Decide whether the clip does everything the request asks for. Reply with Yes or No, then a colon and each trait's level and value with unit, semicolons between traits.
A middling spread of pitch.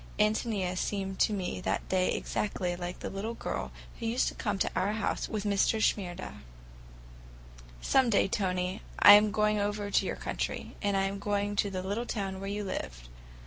No: narrow, 1.9 semitones